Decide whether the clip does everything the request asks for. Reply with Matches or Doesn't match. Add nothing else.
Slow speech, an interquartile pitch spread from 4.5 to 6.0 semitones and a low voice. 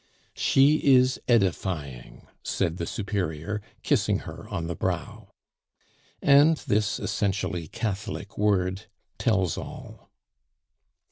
Matches